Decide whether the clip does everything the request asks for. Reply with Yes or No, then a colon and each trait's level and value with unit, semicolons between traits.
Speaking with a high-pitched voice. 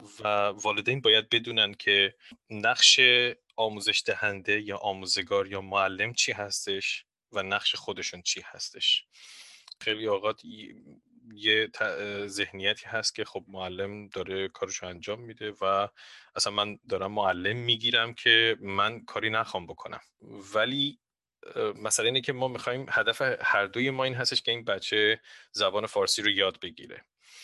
No: low, 110 Hz